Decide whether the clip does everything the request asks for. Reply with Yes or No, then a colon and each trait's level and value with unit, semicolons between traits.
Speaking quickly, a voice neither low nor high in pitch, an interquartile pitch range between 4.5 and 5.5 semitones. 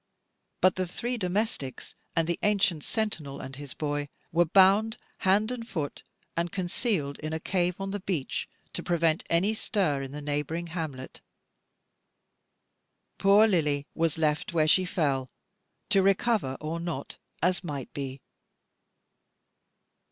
No: slow, 135 wpm; medium, 170 Hz; average, 4.9 semitones